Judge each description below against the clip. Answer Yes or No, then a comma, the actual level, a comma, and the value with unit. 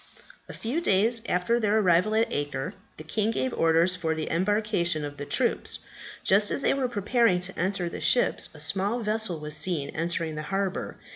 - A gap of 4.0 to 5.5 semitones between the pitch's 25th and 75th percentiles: Yes, average, 5.0 semitones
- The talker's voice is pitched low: No, high, 190 Hz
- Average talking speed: Yes, average, 190 wpm